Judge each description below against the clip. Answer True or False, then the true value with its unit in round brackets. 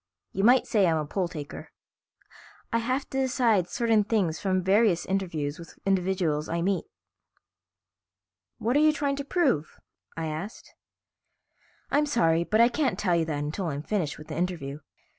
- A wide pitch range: True (6.3 semitones)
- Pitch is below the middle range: False (190 Hz)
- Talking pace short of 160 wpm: False (165 wpm)